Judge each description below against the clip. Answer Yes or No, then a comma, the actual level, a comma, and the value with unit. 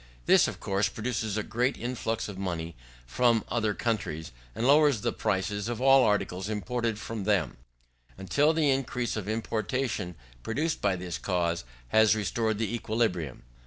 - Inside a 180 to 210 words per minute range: No, average, 155 wpm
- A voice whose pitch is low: Yes, low, 110 Hz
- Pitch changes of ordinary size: Yes, average, 3.8 semitones